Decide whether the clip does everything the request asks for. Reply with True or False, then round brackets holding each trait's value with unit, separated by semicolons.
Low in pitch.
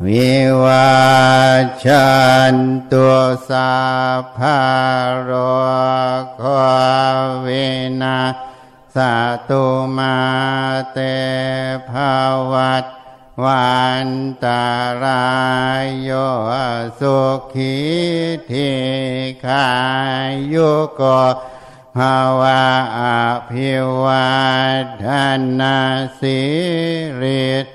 True (130 Hz)